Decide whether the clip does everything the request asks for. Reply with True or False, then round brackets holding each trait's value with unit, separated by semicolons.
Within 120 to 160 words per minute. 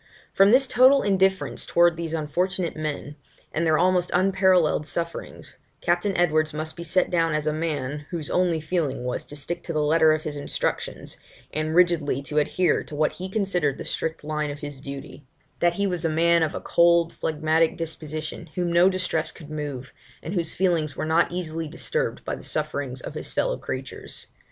False (190 wpm)